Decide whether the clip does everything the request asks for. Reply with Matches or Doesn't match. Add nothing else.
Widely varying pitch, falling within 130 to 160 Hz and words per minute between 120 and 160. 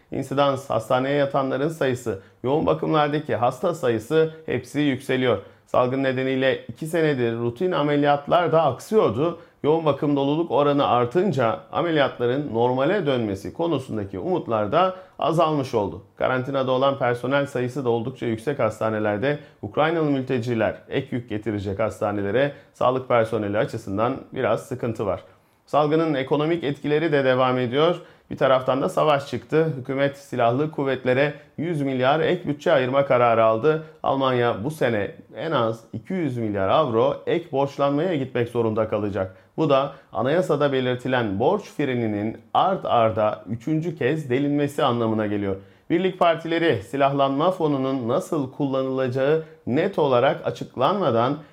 Doesn't match